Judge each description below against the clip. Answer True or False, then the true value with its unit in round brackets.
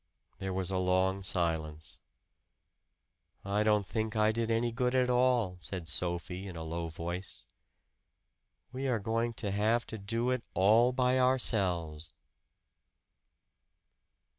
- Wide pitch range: False (4.6 semitones)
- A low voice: True (100 Hz)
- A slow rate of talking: True (130 wpm)